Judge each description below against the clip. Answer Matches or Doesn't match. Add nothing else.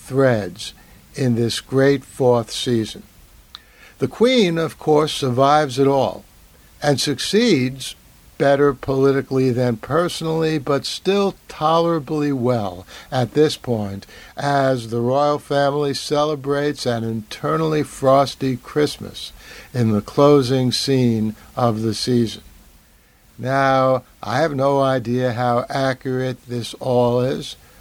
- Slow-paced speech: Matches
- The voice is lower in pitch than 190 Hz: Matches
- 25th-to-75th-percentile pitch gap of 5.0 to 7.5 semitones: Doesn't match